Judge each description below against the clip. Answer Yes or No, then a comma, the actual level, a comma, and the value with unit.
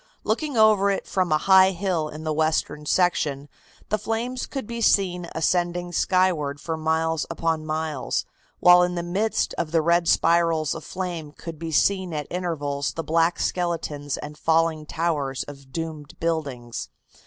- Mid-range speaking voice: Yes, medium, 165 Hz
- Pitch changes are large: No, average, 2.7 semitones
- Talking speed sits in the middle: Yes, average, 160 wpm